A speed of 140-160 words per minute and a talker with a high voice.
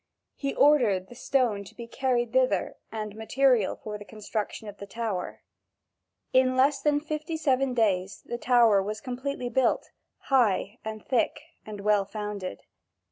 Yes: average, 155 wpm; high, 235 Hz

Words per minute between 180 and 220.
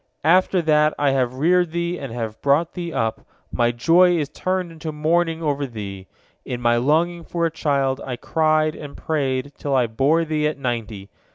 Yes: average, 185 wpm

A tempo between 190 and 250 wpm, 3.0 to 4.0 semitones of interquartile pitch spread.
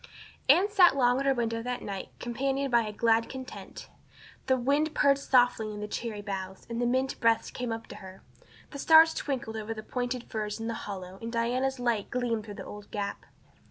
Yes: fast, 205 wpm; average, 3.5 semitones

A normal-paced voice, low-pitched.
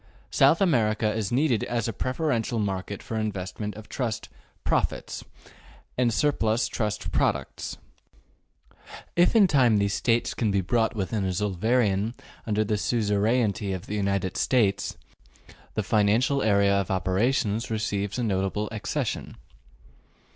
No: slow, 130 wpm; low, 110 Hz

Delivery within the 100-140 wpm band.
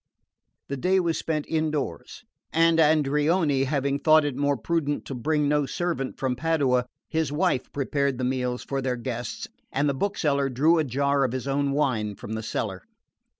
No: average, 175 wpm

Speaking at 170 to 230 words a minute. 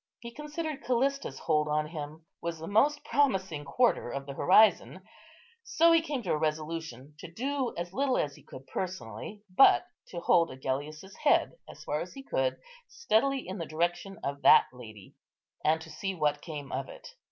Yes: average, 180 wpm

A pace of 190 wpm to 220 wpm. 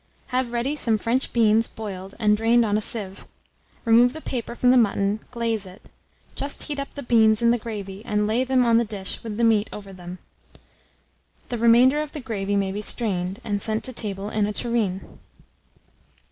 Yes: average, 195 wpm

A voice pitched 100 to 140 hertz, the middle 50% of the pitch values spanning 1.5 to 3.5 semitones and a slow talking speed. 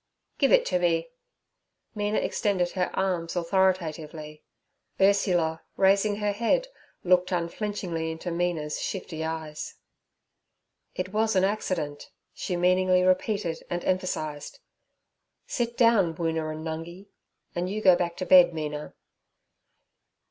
No: medium, 180 Hz; average, 3.1 semitones; slow, 120 wpm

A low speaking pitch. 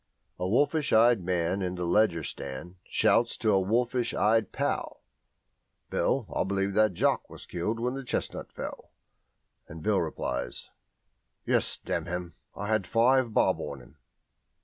Yes: low, 100 Hz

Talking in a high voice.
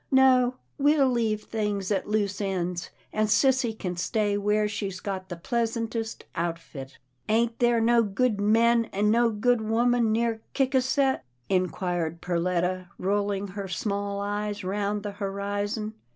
Yes: high, 210 Hz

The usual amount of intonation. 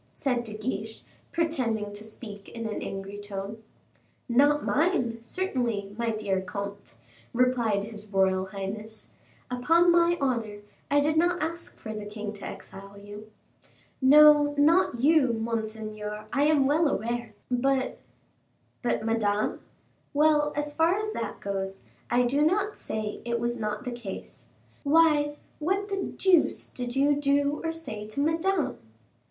No: wide, 5.9 semitones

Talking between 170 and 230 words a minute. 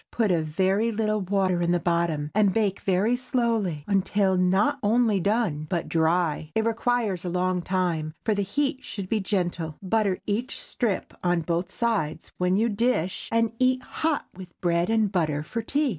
Yes: average, 175 wpm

